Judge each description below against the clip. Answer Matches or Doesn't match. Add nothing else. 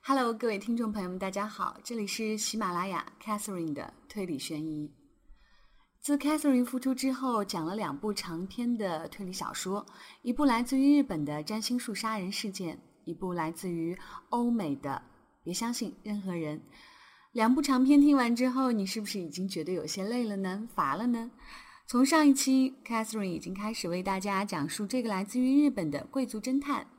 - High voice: Matches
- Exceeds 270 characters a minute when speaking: Matches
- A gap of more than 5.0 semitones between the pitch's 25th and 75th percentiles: Matches